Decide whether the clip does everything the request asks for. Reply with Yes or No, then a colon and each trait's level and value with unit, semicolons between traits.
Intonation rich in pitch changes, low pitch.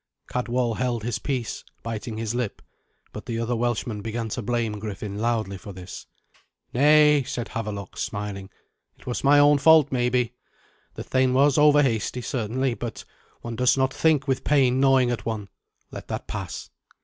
No: average, 3.0 semitones; low, 120 Hz